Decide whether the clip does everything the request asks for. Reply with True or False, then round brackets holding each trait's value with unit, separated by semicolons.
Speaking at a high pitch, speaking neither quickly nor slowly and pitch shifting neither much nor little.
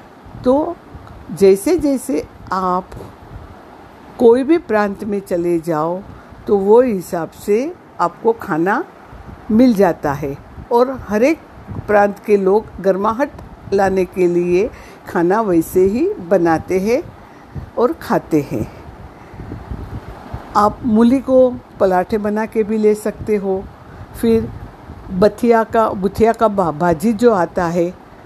True (210 Hz; 120 wpm; 4.0 semitones)